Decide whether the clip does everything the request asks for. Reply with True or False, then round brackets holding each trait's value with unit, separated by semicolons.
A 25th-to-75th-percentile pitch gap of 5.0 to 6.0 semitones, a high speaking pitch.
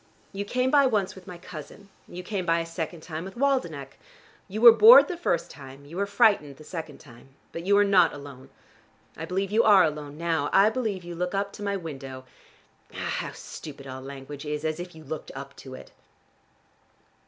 False (5.5 semitones; 170 Hz)